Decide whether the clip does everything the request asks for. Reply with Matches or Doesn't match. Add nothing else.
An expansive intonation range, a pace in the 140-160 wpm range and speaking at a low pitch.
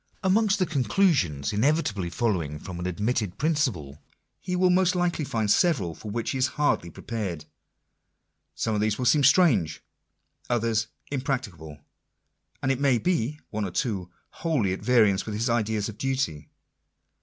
Matches